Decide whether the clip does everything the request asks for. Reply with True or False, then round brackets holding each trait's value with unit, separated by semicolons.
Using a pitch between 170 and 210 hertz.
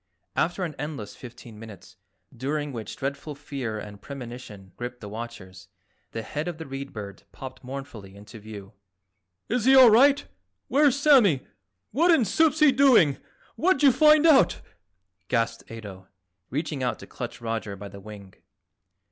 False (130 Hz)